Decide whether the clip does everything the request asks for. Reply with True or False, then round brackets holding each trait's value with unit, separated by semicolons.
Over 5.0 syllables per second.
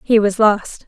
False (3.9 syllables/s)